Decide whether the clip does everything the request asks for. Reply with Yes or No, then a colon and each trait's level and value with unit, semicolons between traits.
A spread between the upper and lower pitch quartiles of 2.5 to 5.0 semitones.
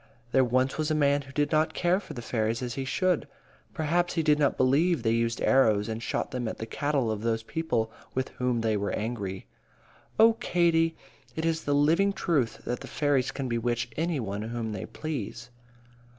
No: wide, 5.4 semitones